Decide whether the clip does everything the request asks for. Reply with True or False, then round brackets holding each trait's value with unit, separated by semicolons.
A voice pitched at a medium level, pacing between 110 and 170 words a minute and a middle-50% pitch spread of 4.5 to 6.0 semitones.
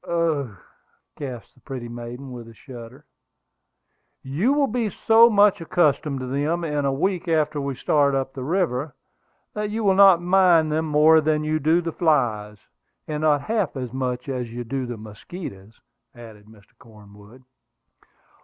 True (145 Hz; 165 wpm; 5.5 semitones)